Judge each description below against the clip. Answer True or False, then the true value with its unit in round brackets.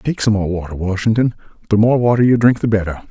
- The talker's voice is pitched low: True (110 Hz)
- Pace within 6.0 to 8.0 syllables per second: True (6.4 syllables/s)